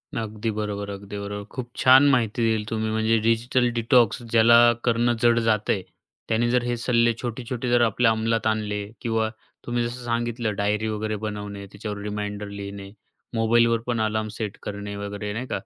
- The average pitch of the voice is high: No, low, 110 Hz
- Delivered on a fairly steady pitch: Yes, narrow, 2.3 semitones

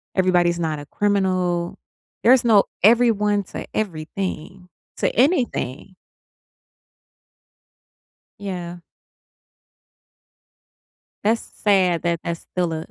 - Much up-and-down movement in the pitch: No, average, 3.2 semitones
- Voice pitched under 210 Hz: Yes, medium, 185 Hz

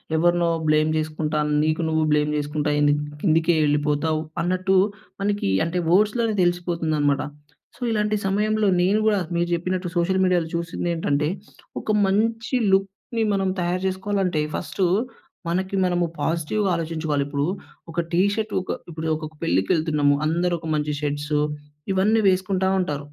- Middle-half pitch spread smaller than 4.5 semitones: Yes, average, 3.7 semitones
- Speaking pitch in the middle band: Yes, medium, 170 Hz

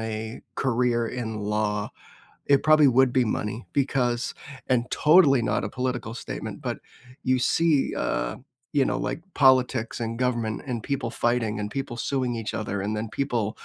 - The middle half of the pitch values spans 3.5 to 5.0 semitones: No, average, 3.1 semitones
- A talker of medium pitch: No, low, 120 Hz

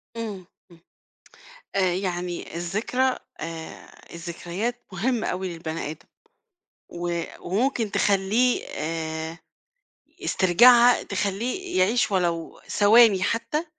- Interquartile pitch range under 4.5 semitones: No, average, 5.2 semitones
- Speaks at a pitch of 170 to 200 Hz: Yes, high, 190 Hz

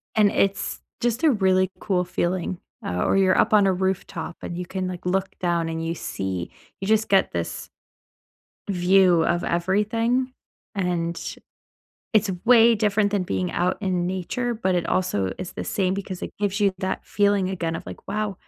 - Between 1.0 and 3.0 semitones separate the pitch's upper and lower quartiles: Yes, average, 2.7 semitones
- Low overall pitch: No, high, 190 Hz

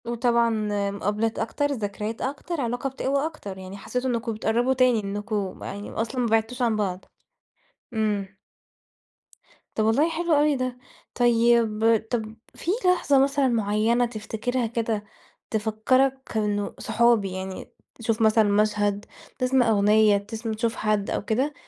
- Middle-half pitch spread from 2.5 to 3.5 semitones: Yes, average, 2.9 semitones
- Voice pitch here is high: Yes, high, 225 Hz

